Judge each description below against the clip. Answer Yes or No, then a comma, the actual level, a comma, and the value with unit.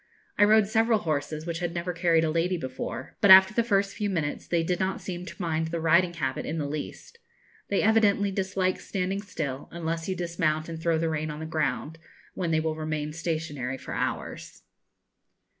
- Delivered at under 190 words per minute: No, average, 195 wpm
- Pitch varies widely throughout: No, average, 3.2 semitones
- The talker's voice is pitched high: No, medium, 170 Hz